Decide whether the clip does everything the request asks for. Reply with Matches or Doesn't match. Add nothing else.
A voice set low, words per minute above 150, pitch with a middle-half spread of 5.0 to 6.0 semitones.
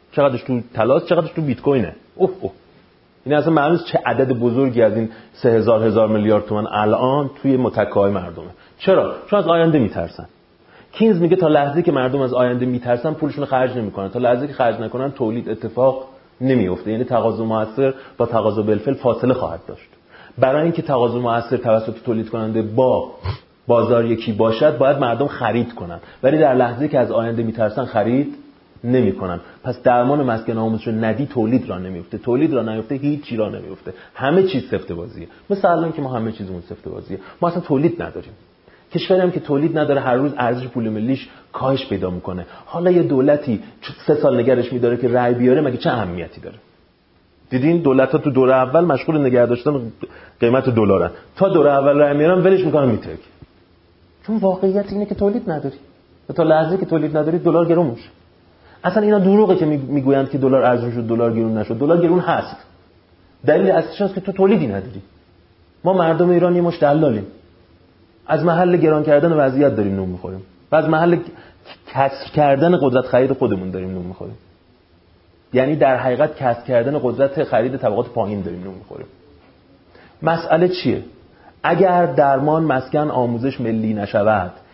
Matches